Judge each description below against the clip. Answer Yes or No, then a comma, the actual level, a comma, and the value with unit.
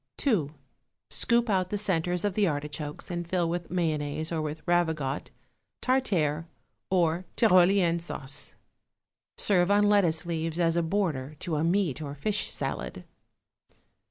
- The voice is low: No, medium, 170 Hz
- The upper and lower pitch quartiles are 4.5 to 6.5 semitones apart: No, average, 3.4 semitones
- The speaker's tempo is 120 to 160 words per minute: Yes, slow, 135 wpm